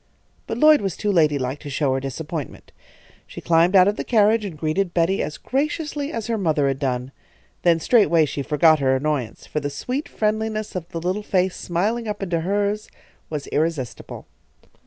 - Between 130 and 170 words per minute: No, average, 180 wpm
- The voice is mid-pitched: Yes, medium, 170 Hz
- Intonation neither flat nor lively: No, wide, 5.9 semitones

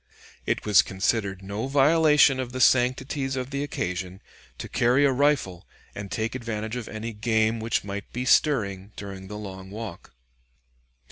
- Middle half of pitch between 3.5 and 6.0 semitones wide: Yes, average, 4.7 semitones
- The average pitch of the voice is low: Yes, low, 110 Hz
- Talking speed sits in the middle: Yes, average, 155 wpm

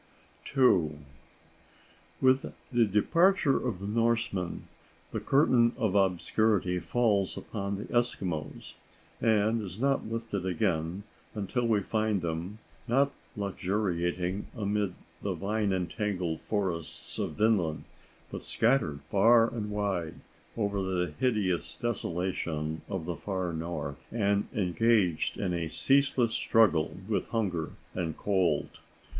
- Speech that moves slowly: Yes, slow, 115 wpm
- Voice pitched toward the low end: Yes, low, 100 Hz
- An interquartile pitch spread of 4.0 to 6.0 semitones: Yes, average, 4.3 semitones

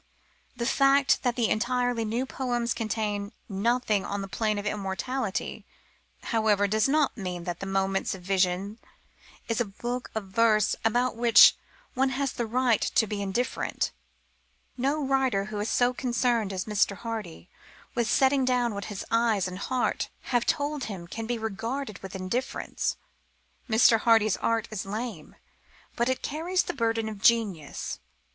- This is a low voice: No, high, 225 Hz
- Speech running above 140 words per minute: Yes, average, 155 wpm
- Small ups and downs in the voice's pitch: No, average, 3.5 semitones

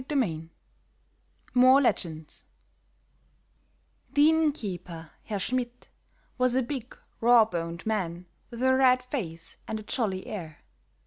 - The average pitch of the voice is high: Yes, high, 225 Hz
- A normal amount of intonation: No, wide, 7.0 semitones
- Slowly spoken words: Yes, slow, 125 wpm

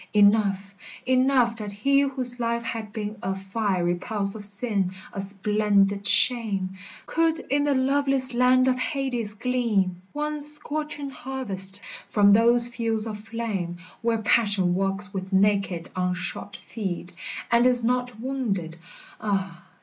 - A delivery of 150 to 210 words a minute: No, slow, 135 wpm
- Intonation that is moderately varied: Yes, average, 4.3 semitones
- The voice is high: Yes, high, 220 Hz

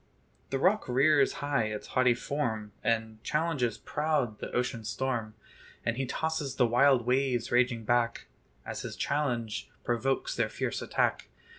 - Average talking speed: Yes, average, 145 wpm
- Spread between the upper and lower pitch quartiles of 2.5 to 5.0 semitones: Yes, average, 3.2 semitones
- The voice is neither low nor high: No, low, 125 Hz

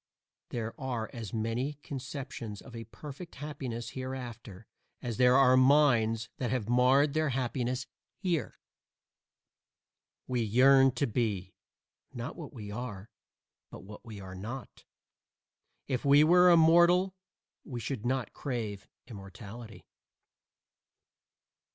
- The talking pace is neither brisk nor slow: No, slow, 115 wpm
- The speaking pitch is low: Yes, low, 125 Hz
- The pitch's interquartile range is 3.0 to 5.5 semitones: Yes, average, 3.5 semitones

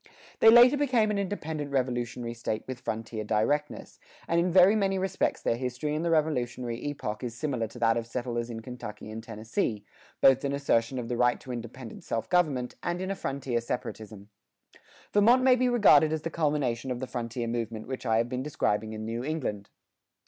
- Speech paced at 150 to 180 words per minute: No, average, 190 wpm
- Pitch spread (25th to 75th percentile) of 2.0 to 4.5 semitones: No, wide, 5.5 semitones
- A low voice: Yes, low, 125 Hz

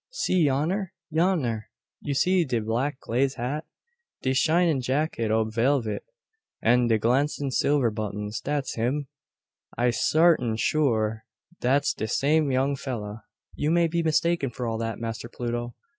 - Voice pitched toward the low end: Yes, low, 130 Hz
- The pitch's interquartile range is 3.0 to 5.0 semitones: Yes, average, 4.6 semitones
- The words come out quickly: No, average, 145 wpm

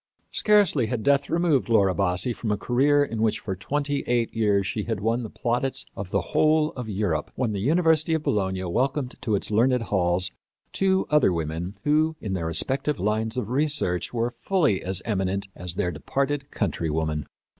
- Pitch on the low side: Yes, low, 115 Hz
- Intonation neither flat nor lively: No, wide, 6.7 semitones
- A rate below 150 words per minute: No, average, 180 wpm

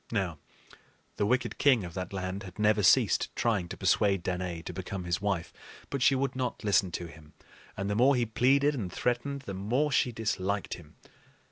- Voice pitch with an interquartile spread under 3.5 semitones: No, average, 5.2 semitones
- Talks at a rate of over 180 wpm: Yes, average, 195 wpm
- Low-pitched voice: Yes, low, 100 Hz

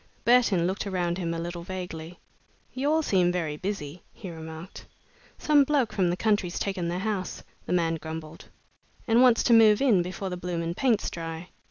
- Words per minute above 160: Yes, average, 180 wpm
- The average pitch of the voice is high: No, medium, 180 Hz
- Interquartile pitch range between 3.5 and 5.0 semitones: Yes, average, 4.0 semitones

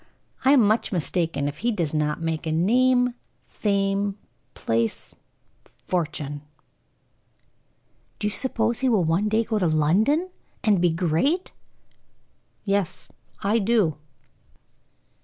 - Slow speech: Yes, slow, 120 wpm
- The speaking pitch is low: No, high, 195 Hz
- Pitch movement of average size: No, wide, 5.9 semitones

